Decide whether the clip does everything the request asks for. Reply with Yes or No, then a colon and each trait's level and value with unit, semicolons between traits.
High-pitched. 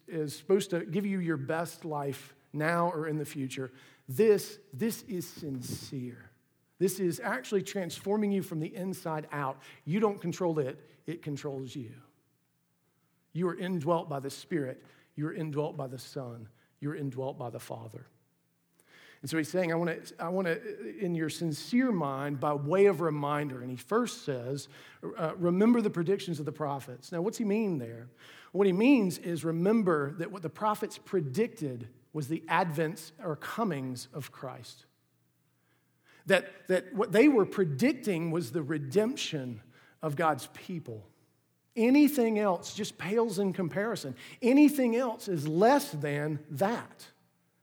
No: medium, 160 Hz